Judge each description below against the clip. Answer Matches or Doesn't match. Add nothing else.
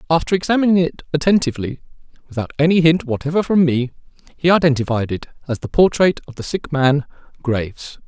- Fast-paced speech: Doesn't match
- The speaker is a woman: Doesn't match